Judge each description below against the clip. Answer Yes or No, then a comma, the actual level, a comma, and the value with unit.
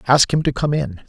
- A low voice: Yes, low, 130 Hz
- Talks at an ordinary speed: No, fast, 280 wpm